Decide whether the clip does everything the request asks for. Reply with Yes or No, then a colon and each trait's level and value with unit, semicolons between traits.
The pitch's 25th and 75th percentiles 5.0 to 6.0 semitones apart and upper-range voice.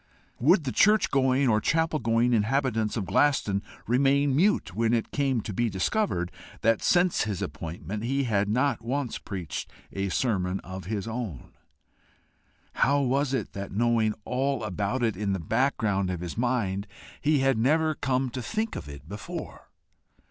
No: wide, 5.4 semitones; low, 115 Hz